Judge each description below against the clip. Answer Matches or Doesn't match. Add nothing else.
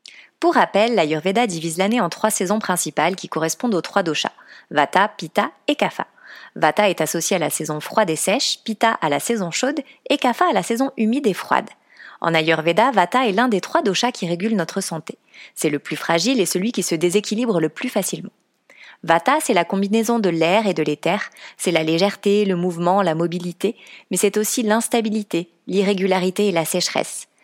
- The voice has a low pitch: Doesn't match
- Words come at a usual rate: Matches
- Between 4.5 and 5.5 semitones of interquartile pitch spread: Matches